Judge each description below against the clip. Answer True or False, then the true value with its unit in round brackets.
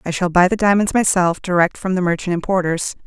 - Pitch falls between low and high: True (180 Hz)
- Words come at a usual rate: False (215 wpm)